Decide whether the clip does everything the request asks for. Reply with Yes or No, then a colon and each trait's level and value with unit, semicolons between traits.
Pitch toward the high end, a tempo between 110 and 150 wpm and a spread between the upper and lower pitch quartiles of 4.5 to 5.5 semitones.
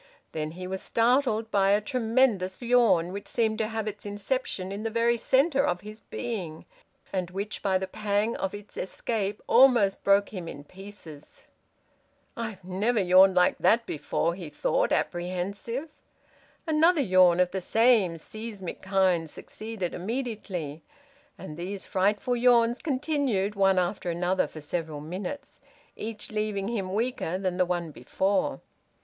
No: high, 200 Hz; average, 145 wpm; average, 3.9 semitones